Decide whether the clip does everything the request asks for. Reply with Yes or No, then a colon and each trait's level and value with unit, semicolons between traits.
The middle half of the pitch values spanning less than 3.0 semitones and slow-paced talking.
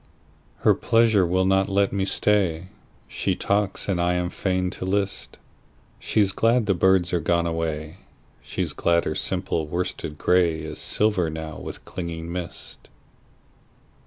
Yes: narrow, 2.6 semitones; slow, 130 wpm